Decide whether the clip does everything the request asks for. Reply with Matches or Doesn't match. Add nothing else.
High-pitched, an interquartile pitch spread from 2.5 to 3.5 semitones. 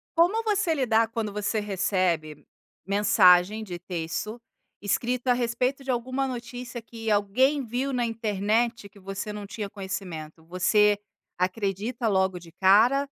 Doesn't match